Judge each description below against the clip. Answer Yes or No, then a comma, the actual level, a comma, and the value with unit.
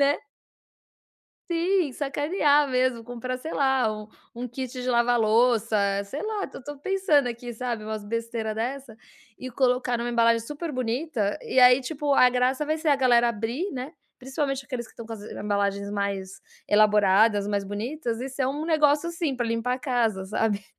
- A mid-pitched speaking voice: No, very high, 250 Hz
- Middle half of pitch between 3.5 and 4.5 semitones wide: Yes, average, 3.8 semitones